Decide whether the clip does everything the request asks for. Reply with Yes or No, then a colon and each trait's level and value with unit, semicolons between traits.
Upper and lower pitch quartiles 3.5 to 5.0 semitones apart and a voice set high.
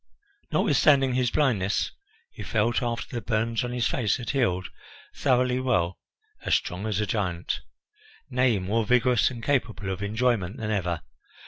No: average, 3.8 semitones; low, 115 Hz